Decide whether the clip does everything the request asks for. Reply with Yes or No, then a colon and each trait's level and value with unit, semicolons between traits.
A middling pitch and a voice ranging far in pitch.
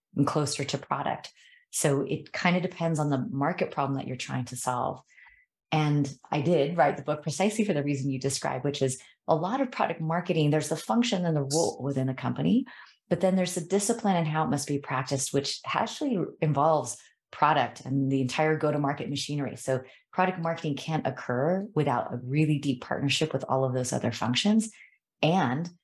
No: medium, 150 Hz; average, 4.5 semitones